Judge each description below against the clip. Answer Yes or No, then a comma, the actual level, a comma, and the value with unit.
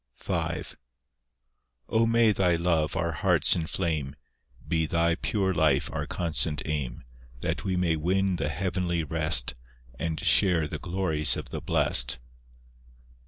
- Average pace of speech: No, slow, 130 wpm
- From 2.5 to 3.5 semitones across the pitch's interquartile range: Yes, average, 3.1 semitones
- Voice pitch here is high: No, very low, 85 Hz